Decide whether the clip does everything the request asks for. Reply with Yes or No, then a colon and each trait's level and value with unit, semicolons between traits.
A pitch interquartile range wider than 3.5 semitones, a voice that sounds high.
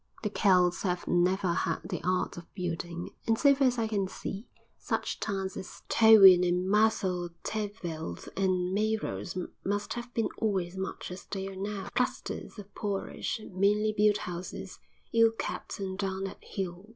No: average, 2.8 semitones; high, 195 Hz